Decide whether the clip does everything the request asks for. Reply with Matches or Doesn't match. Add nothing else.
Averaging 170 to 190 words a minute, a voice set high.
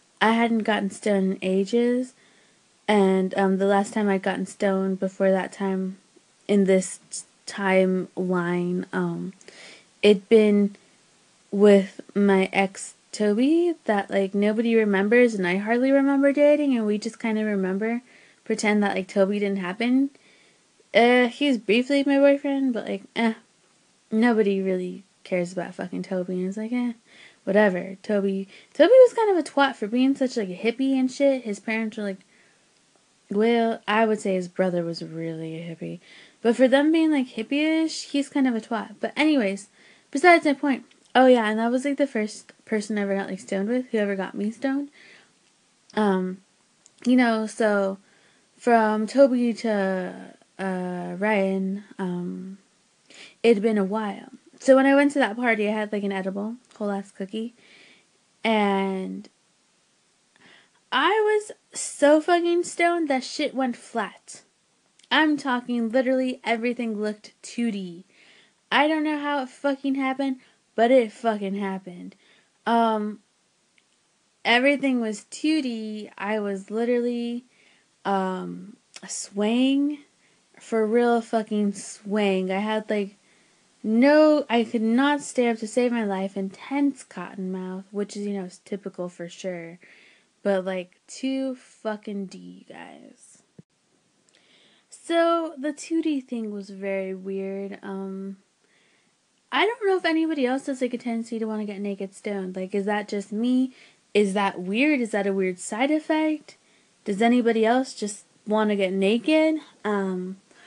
Doesn't match